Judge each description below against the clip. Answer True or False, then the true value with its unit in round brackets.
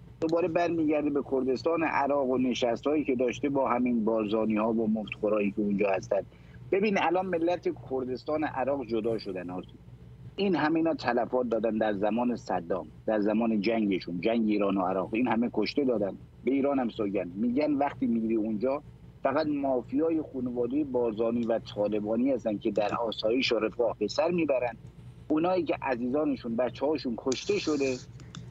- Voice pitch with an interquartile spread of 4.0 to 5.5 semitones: True (5.0 semitones)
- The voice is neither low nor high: False (125 Hz)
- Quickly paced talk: False (155 wpm)